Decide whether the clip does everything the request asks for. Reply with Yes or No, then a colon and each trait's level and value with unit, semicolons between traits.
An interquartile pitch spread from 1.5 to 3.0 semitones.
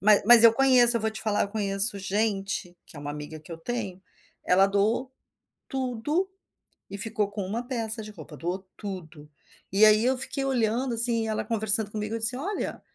No: average, 3.4 semitones